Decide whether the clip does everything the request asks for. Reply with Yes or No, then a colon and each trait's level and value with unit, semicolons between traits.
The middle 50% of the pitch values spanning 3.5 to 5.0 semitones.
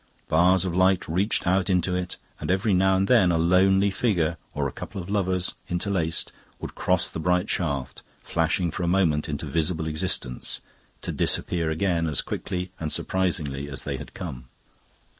No: average, 2.9 semitones